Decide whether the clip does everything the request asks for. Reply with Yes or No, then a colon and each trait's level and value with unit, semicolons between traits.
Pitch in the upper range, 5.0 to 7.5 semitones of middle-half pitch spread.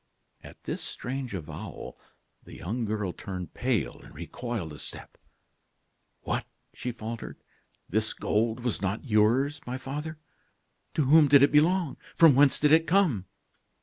No: low, 125 Hz; average, 5.3 semitones